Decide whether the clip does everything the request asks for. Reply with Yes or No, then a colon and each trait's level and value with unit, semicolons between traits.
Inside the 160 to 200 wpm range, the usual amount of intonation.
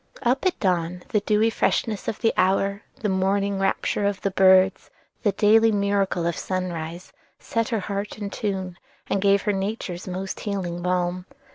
No: average, 165 wpm; narrow, 2.1 semitones